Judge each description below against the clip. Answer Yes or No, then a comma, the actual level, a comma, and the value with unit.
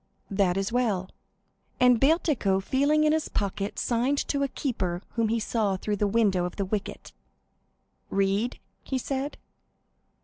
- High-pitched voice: Yes, high, 220 Hz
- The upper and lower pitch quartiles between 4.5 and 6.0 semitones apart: Yes, average, 5.2 semitones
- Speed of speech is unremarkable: Yes, average, 145 wpm